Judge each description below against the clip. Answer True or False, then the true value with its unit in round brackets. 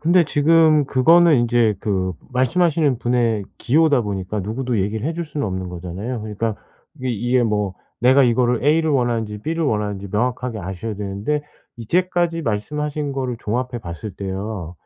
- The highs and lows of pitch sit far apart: True (5.9 semitones)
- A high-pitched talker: False (120 Hz)